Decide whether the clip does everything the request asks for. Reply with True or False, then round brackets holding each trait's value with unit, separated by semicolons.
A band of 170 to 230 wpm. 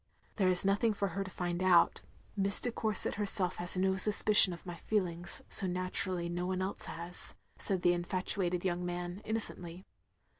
True (180 wpm)